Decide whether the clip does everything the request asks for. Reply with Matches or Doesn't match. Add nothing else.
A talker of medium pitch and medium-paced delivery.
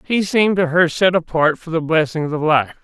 Doesn't match